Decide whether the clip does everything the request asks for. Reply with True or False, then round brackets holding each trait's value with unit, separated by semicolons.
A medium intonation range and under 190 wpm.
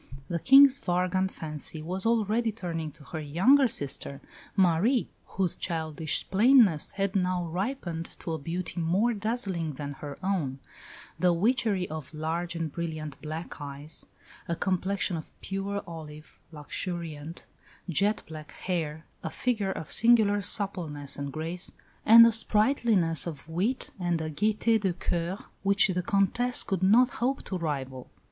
True (4.4 semitones; 145 wpm)